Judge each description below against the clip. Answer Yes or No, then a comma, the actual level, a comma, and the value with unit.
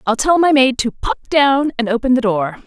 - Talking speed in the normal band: No, fast, 245 wpm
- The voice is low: No, very high, 250 Hz